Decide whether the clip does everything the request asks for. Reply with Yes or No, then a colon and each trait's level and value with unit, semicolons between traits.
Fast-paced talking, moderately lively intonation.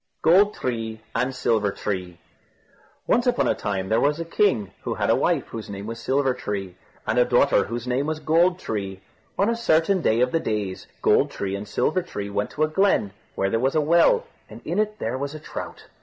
No: fast, 215 wpm; wide, 7.8 semitones